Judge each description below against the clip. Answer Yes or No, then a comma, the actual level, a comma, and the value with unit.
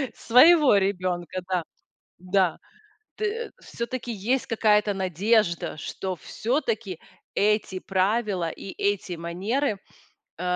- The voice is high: Yes, high, 200 Hz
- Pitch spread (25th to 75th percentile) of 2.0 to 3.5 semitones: No, average, 4.0 semitones